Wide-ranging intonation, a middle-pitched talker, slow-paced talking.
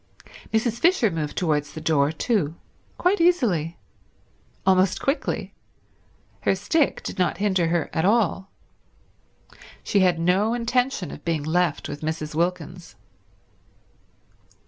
Yes: wide, 5.8 semitones; medium, 180 Hz; slow, 120 wpm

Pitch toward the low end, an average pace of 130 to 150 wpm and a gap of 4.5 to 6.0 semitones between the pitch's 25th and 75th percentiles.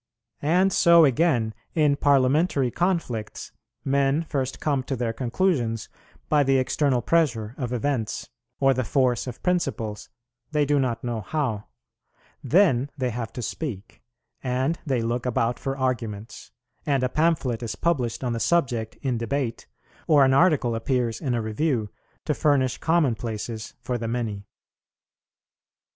No: low, 130 Hz; average, 145 wpm; average, 3.9 semitones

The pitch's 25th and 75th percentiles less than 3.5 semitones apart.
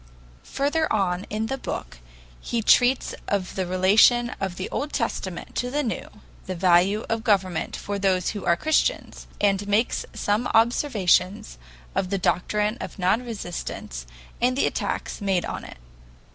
No: average, 4.3 semitones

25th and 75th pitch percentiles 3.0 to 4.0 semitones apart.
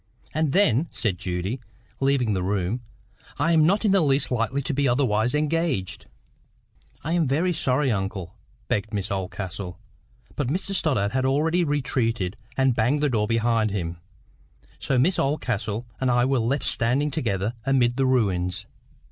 No: wide, 5.6 semitones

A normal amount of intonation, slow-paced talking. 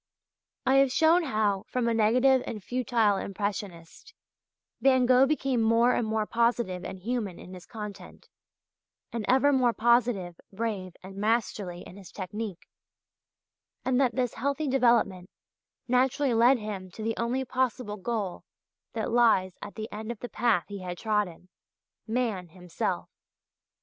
No: average, 4.2 semitones; average, 145 wpm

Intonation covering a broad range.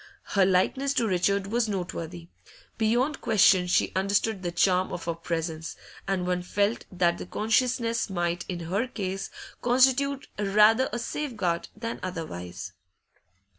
No: average, 4.6 semitones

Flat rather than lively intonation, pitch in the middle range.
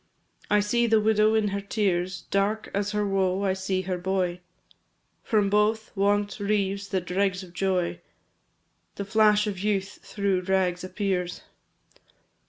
No: narrow, 1.9 semitones; high, 195 Hz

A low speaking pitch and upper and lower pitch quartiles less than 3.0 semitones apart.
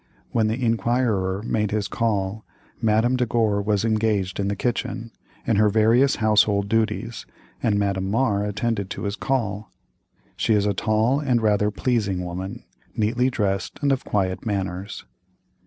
Yes: low, 105 Hz; narrow, 2.4 semitones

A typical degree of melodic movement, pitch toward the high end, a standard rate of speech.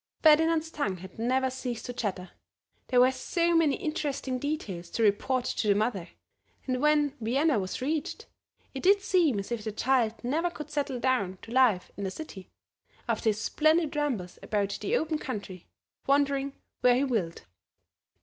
No: wide, 5.9 semitones; very high, 255 Hz; average, 170 wpm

